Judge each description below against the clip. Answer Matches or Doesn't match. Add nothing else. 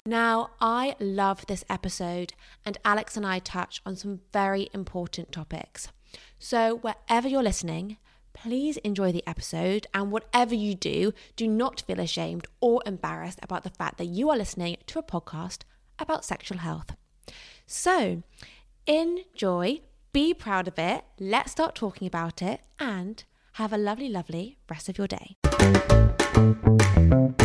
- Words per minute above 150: Doesn't match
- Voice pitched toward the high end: Matches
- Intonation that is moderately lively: Matches